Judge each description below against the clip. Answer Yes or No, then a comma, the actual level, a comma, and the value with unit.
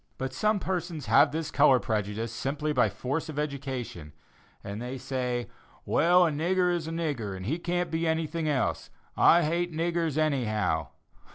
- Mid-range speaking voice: Yes, medium, 150 Hz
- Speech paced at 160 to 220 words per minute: Yes, average, 170 wpm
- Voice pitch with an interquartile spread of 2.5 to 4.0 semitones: No, average, 5.1 semitones